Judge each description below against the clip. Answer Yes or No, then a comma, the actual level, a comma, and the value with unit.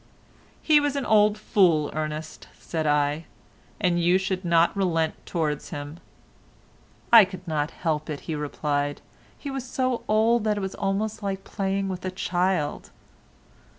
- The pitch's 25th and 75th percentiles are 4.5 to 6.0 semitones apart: Yes, average, 4.9 semitones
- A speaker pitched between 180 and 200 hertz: Yes, medium, 185 Hz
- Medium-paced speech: Yes, average, 150 wpm